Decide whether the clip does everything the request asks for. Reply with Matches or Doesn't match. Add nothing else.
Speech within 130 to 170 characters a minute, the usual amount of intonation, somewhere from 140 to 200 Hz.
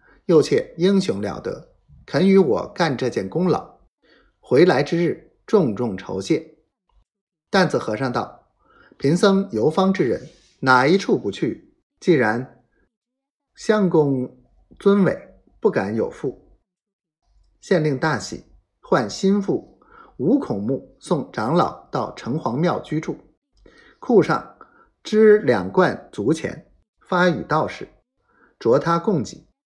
Matches